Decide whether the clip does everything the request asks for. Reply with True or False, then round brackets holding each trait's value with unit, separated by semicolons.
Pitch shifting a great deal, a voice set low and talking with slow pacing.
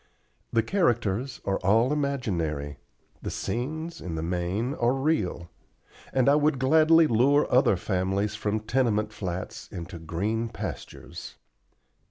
True (6.5 semitones; 110 Hz; 125 wpm)